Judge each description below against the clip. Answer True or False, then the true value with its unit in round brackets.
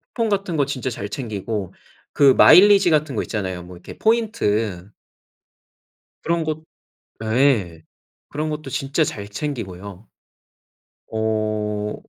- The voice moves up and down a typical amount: False (7.0 semitones)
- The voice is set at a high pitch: False (115 Hz)